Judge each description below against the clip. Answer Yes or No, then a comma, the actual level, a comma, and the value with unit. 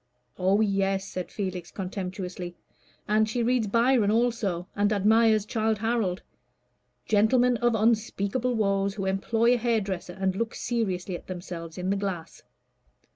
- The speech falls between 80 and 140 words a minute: Yes, slow, 135 wpm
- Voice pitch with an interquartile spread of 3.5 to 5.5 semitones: No, average, 3.1 semitones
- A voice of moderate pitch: No, high, 205 Hz